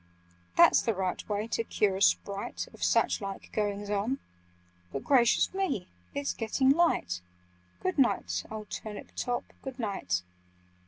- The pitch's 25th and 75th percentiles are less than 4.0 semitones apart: No, average, 4.3 semitones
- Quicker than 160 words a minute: No, average, 145 wpm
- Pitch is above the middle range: Yes, high, 205 Hz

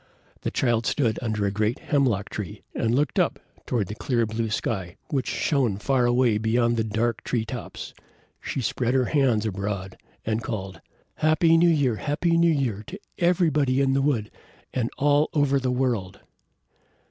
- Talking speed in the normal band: Yes, average, 170 wpm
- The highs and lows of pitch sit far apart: No, average, 4.3 semitones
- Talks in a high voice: No, low, 120 Hz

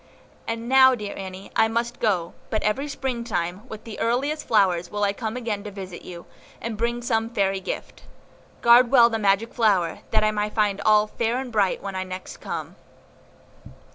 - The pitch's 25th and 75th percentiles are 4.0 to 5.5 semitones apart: No, average, 3.1 semitones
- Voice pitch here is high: Yes, high, 215 Hz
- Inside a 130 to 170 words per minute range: No, average, 185 wpm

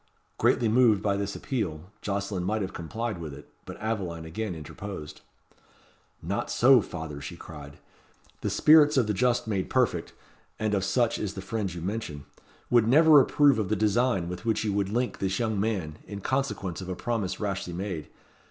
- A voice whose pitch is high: No, low, 100 Hz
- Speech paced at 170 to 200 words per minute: Yes, average, 180 wpm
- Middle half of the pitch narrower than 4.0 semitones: No, average, 4.3 semitones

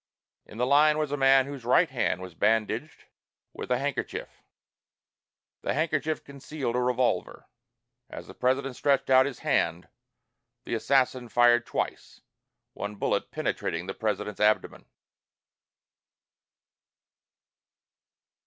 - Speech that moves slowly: Yes, slow, 115 wpm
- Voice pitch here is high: No, low, 125 Hz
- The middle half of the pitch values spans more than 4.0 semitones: No, average, 3.7 semitones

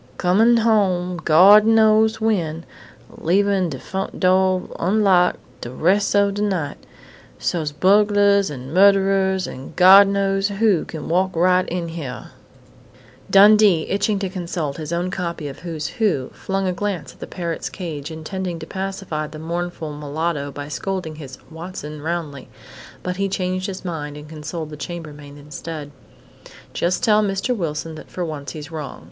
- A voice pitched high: No, medium, 180 Hz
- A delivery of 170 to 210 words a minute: No, average, 155 wpm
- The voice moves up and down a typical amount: Yes, average, 4.0 semitones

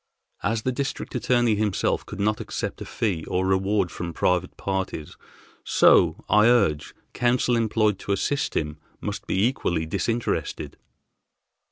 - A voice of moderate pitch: No, low, 105 Hz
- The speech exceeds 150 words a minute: No, average, 140 wpm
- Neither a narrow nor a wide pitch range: Yes, average, 4.4 semitones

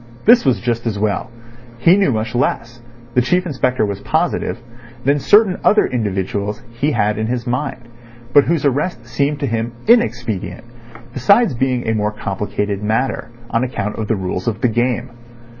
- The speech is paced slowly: No, average, 160 wpm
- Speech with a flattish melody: No, average, 3.6 semitones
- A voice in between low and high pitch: No, low, 120 Hz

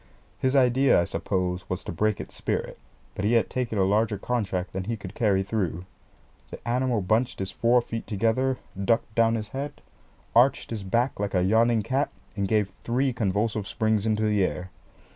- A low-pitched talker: Yes, low, 110 Hz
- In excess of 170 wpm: Yes, average, 185 wpm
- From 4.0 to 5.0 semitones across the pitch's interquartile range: No, average, 3.5 semitones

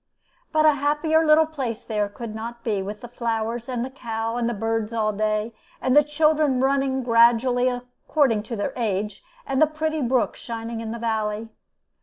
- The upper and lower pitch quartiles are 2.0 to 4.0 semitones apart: Yes, average, 3.4 semitones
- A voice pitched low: No, high, 235 Hz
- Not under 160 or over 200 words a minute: Yes, average, 185 wpm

